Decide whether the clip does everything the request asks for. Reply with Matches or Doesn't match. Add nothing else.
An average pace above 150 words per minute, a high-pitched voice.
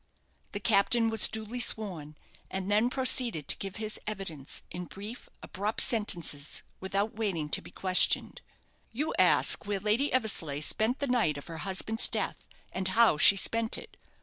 Matches